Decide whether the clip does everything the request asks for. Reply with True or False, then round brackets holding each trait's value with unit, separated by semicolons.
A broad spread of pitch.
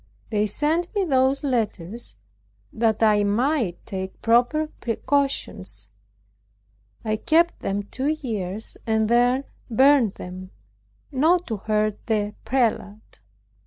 False (4.8 semitones)